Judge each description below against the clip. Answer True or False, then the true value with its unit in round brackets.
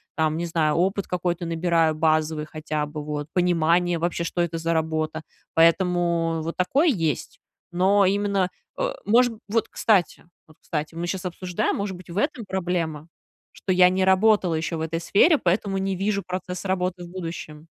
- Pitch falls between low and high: True (175 Hz)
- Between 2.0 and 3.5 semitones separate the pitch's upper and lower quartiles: True (2.7 semitones)